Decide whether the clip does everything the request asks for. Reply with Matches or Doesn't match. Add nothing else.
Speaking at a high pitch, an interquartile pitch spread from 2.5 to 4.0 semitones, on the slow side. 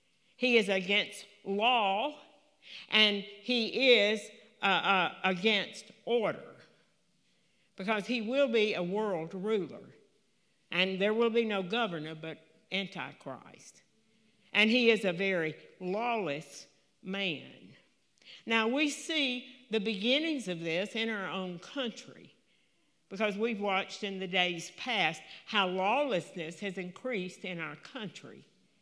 Matches